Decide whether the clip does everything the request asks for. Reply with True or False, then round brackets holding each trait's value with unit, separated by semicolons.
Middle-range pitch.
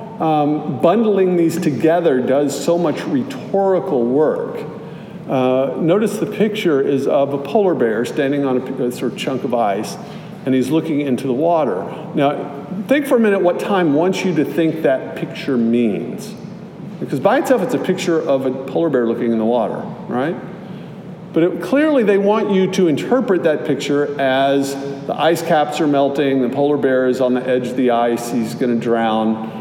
True (155 Hz)